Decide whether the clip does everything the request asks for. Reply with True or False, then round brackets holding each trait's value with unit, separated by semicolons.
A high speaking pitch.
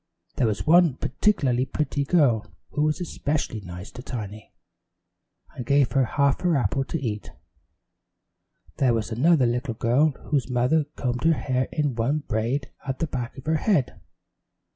False (130 Hz)